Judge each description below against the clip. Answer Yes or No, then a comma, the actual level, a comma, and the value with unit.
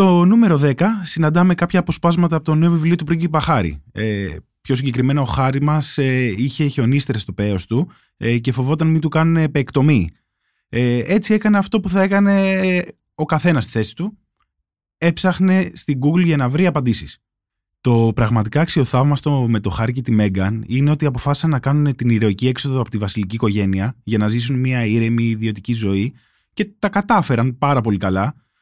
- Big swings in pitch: Yes, wide, 6.4 semitones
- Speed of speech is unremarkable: No, fast, 180 wpm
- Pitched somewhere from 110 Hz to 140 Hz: Yes, low, 135 Hz